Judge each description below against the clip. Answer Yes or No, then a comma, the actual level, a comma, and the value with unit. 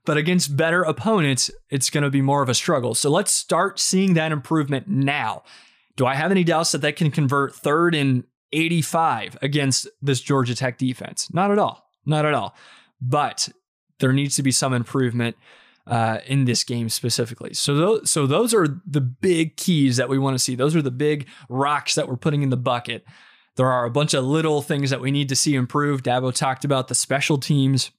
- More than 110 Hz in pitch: Yes, medium, 140 Hz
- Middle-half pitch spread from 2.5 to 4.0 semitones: Yes, average, 3.2 semitones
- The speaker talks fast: Yes, fast, 210 wpm